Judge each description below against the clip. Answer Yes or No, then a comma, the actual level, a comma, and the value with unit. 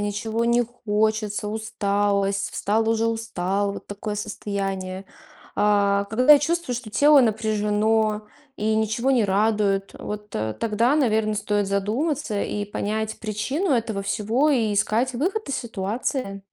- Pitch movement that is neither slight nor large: No, narrow, 2.3 semitones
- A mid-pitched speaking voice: No, high, 215 Hz